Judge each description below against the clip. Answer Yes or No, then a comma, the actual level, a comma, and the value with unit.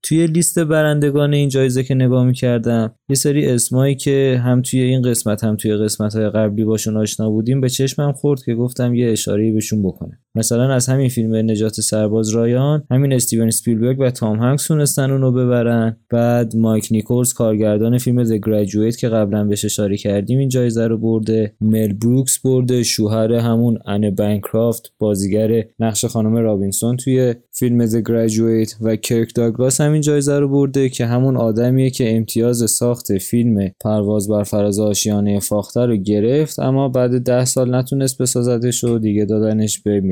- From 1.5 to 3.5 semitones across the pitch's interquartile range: Yes, average, 2.8 semitones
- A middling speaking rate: No, fast, 165 wpm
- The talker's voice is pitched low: Yes, low, 115 Hz